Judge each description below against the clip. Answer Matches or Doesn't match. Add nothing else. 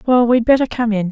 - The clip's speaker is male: Doesn't match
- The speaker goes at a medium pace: Doesn't match